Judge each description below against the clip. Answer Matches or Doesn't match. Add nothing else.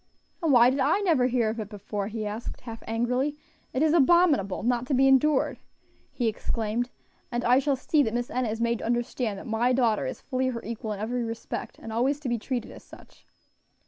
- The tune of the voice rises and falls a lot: Doesn't match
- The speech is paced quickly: Matches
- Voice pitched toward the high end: Matches